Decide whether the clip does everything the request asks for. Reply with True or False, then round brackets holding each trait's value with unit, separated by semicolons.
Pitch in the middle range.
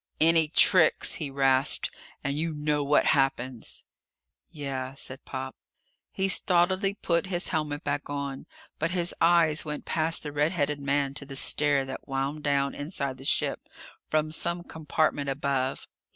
True (145 Hz)